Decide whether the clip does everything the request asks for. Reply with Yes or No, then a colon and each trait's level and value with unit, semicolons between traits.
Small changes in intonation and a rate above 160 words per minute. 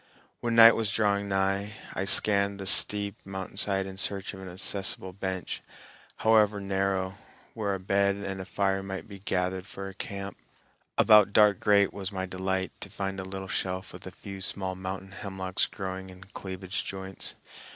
Yes: narrow, 1.1 semitones; average, 170 wpm